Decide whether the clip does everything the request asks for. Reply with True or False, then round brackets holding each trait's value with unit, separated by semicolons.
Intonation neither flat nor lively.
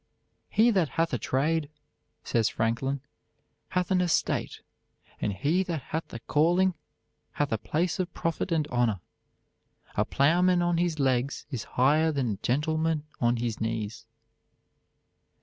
False (5.7 semitones)